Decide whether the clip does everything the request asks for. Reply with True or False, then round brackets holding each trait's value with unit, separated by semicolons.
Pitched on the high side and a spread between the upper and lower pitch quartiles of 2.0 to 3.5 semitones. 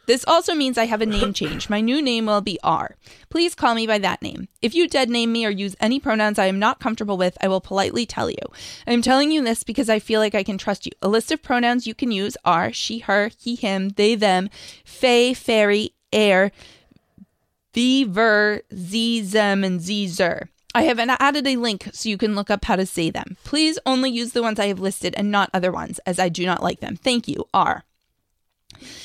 True (220 Hz; 3.2 semitones)